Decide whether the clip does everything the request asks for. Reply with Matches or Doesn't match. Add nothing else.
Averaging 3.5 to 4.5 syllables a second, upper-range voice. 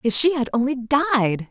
Matches